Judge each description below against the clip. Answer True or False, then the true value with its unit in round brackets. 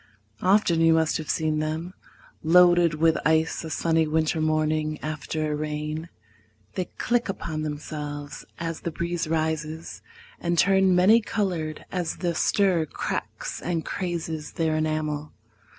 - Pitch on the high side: False (160 Hz)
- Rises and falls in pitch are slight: True (1.9 semitones)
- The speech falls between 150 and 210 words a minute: False (135 wpm)